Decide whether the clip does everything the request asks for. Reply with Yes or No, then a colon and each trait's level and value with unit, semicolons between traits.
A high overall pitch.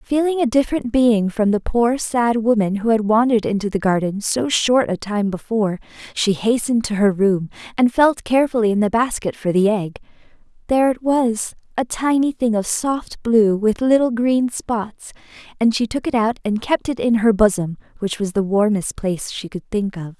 Yes: high, 225 Hz